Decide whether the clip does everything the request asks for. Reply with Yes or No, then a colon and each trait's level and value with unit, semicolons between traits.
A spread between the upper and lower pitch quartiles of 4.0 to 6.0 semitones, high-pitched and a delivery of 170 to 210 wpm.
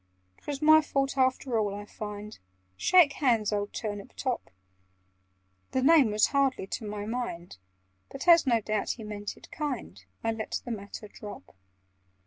No: average, 4.8 semitones; high, 225 Hz; average, 155 wpm